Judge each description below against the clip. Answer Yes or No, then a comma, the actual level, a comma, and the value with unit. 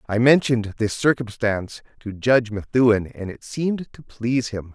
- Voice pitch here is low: Yes, low, 115 Hz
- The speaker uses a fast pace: No, average, 165 wpm